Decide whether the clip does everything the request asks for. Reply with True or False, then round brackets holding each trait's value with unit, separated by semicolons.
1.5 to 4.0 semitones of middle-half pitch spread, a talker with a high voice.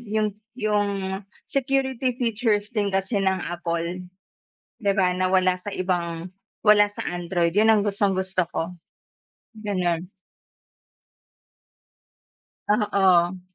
True (2.7 semitones; 195 Hz)